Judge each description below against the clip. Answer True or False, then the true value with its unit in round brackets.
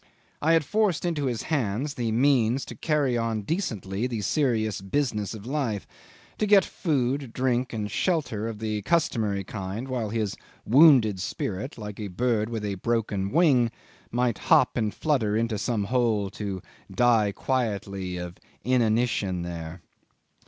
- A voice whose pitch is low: True (115 Hz)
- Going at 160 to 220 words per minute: False (150 wpm)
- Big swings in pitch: False (4.2 semitones)